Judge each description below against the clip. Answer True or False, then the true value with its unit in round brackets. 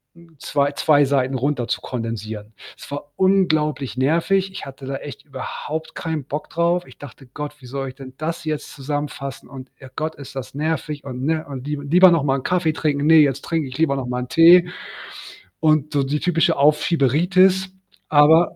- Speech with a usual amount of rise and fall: True (3.2 semitones)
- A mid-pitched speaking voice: True (145 Hz)